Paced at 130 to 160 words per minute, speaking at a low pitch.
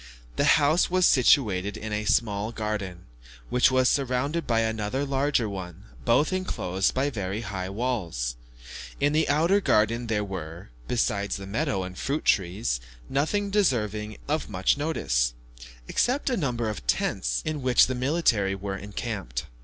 Yes: average, 145 wpm; low, 110 Hz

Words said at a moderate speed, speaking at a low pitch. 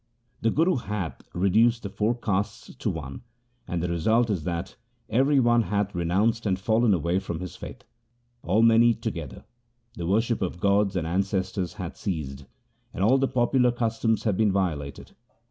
Yes: average, 175 wpm; low, 100 Hz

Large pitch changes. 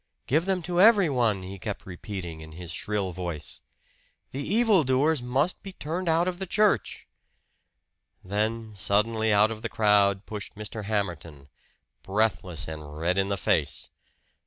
Yes: wide, 7.9 semitones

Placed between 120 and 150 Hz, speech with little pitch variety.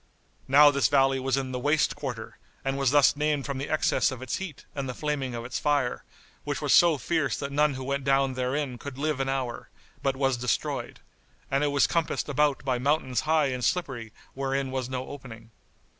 Yes: low, 135 Hz; narrow, 2.1 semitones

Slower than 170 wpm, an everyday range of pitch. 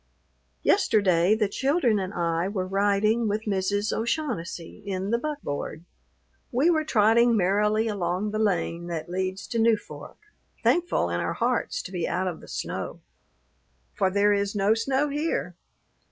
Yes: average, 150 wpm; average, 3.8 semitones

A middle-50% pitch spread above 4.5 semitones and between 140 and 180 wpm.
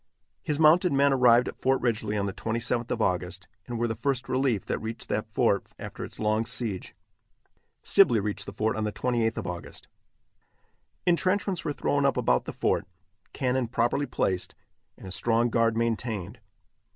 No: average, 3.5 semitones; average, 175 wpm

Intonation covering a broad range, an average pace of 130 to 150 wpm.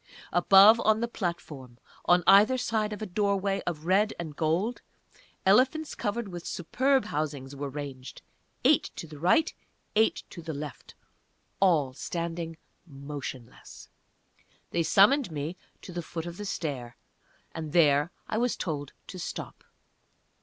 Yes: wide, 5.7 semitones; average, 140 wpm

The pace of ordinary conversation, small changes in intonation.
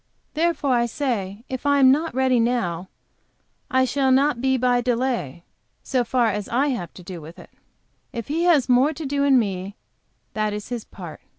No: average, 190 wpm; average, 4.5 semitones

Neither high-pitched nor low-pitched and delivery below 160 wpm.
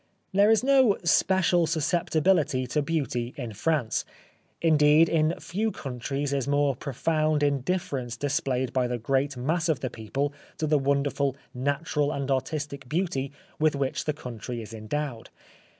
Yes: medium, 145 Hz; average, 145 wpm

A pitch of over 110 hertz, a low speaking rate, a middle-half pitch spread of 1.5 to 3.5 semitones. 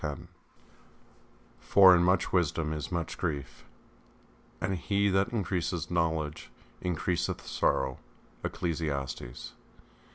No: very low, 85 Hz; slow, 95 wpm; average, 3.2 semitones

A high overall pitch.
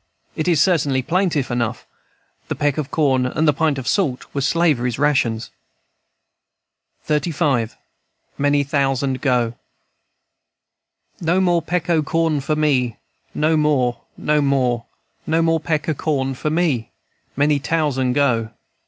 No: medium, 145 Hz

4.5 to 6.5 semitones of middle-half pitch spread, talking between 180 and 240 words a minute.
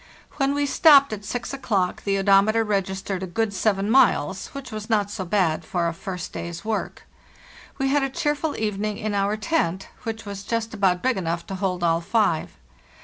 No: average, 3.3 semitones; average, 195 wpm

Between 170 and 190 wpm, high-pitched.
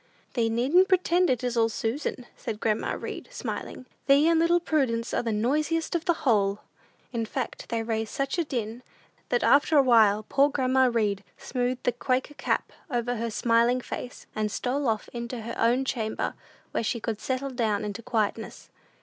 Yes: average, 180 wpm; high, 245 Hz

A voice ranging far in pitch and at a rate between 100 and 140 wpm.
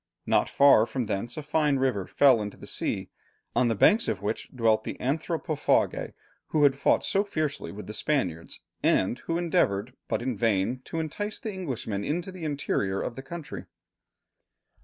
No: wide, 6.3 semitones; average, 175 wpm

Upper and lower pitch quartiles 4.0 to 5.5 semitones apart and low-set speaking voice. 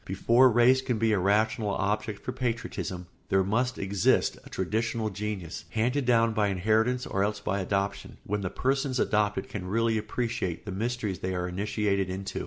No: average, 3.1 semitones; low, 105 Hz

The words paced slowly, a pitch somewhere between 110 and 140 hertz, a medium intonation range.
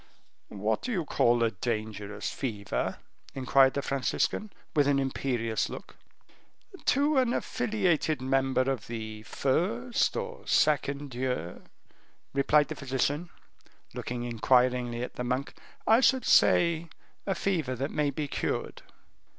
Yes: slow, 125 wpm; low, 135 Hz; average, 5.0 semitones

